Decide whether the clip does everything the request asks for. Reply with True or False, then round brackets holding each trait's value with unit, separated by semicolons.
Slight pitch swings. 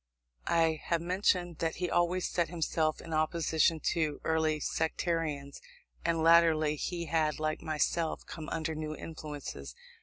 True (1.5 semitones)